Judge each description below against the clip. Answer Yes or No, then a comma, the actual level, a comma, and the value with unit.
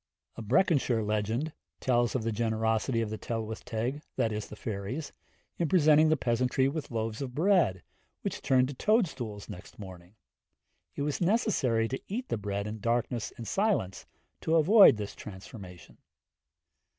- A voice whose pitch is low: Yes, low, 120 Hz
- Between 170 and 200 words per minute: No, average, 140 wpm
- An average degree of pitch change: No, wide, 5.7 semitones